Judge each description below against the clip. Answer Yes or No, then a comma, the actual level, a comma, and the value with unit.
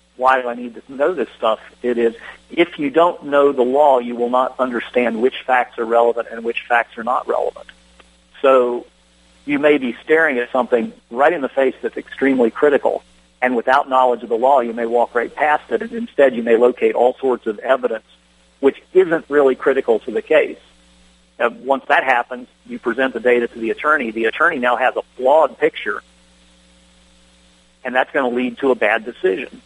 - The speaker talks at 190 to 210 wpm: Yes, average, 200 wpm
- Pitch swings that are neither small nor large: Yes, average, 3.2 semitones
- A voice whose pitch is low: Yes, low, 120 Hz